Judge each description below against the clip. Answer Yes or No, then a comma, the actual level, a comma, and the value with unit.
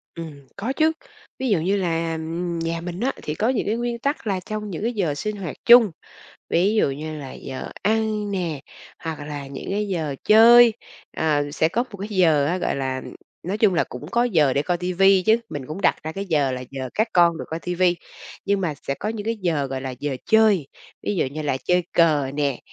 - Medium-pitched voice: Yes, medium, 175 Hz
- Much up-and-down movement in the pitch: Yes, wide, 5.9 semitones